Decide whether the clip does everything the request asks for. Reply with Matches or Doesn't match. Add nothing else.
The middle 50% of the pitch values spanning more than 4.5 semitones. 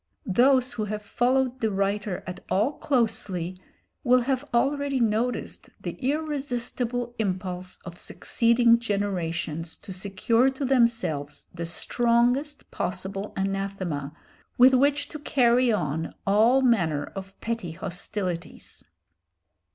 Matches